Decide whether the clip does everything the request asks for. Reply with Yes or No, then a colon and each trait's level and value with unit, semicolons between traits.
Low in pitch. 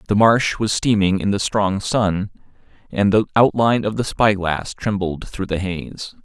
Yes: low, 100 Hz